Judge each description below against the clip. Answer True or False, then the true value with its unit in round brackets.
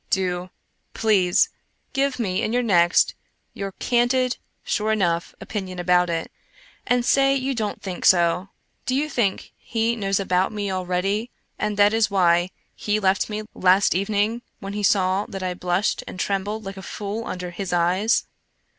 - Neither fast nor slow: True (165 wpm)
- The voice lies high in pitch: True (195 Hz)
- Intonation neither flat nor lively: True (3.1 semitones)